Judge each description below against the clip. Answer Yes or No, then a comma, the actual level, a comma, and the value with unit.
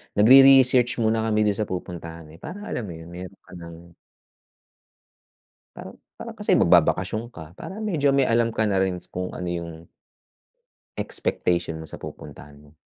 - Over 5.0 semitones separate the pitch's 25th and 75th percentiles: Yes, wide, 5.6 semitones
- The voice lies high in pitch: No, very low, 95 Hz